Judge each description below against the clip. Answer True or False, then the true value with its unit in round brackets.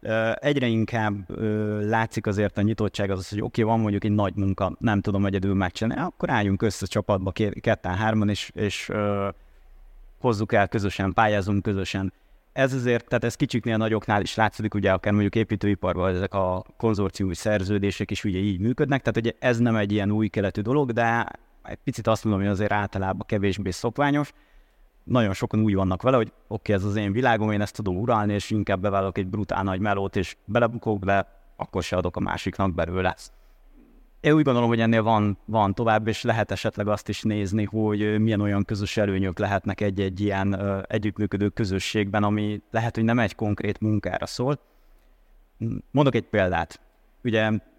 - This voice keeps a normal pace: False (185 wpm)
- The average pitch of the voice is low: True (105 Hz)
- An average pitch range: False (2.3 semitones)